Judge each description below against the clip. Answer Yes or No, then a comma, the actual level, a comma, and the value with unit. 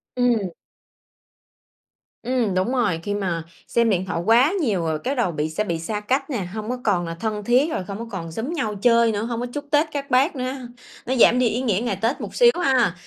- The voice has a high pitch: Yes, high, 230 Hz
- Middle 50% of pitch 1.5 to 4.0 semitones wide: No, average, 4.7 semitones